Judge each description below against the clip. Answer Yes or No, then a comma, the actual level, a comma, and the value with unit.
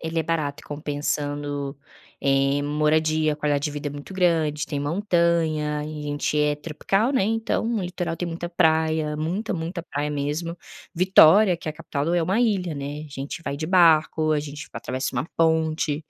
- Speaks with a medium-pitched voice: Yes, medium, 155 Hz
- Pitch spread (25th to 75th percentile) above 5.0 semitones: No, narrow, 2.5 semitones